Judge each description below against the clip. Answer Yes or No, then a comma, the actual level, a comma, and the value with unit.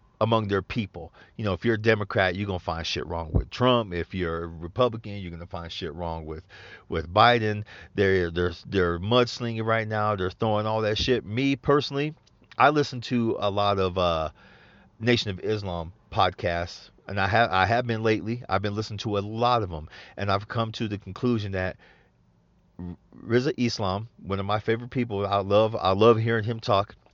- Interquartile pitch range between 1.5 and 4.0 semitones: Yes, average, 3.7 semitones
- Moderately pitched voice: No, low, 105 Hz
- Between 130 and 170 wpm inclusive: No, average, 195 wpm